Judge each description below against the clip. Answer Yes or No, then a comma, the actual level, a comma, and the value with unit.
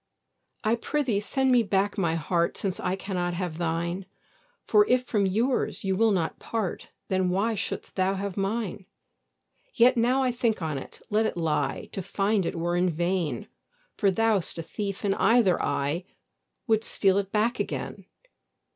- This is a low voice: No, high, 195 Hz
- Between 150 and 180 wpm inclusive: Yes, average, 165 wpm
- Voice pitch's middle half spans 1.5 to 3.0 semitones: No, average, 4.1 semitones